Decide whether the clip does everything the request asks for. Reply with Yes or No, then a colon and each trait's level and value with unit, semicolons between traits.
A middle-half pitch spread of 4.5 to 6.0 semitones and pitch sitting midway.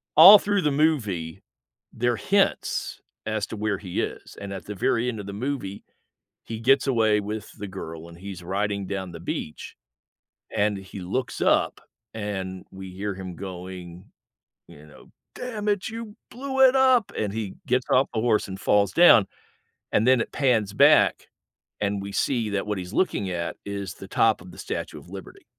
No: average, 5.2 semitones; low, 105 Hz